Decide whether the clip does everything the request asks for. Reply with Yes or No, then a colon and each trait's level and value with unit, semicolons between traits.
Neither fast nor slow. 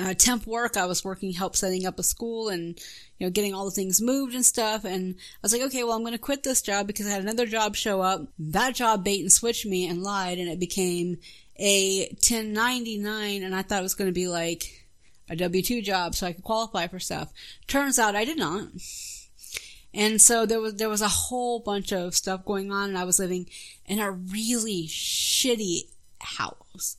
No: fast, 220 wpm